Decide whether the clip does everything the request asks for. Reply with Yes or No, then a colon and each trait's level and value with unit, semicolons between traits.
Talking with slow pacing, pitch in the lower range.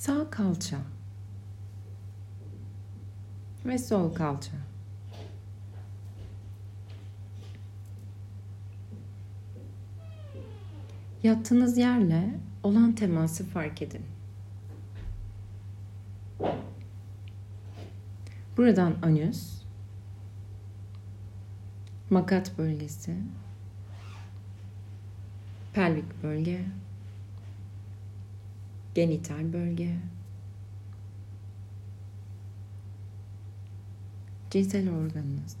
Yes: slow, 35 wpm; low, 100 Hz